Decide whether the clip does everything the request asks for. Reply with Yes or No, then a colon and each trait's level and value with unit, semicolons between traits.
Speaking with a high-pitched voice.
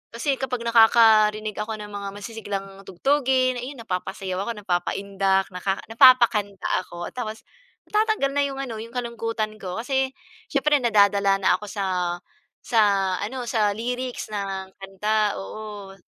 Yes: high, 215 Hz